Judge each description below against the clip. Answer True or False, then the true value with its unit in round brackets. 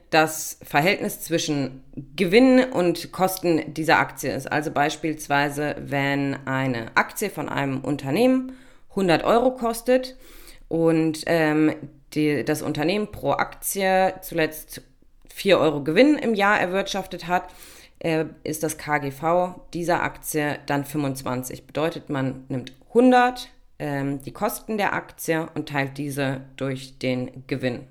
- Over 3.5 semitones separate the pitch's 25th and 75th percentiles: True (4.6 semitones)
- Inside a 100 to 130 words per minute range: True (125 wpm)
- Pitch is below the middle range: False (155 Hz)